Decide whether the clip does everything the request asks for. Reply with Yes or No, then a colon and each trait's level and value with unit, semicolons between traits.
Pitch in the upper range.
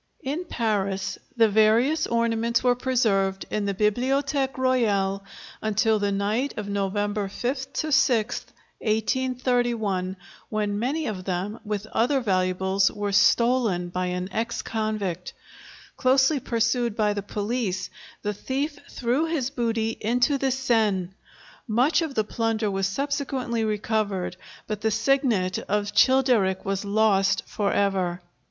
Yes: high, 220 Hz